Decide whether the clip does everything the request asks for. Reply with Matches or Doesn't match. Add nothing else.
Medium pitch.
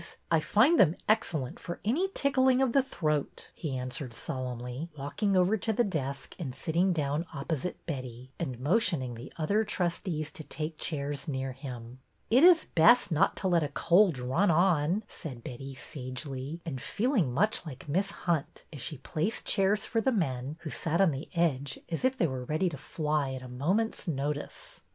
Matches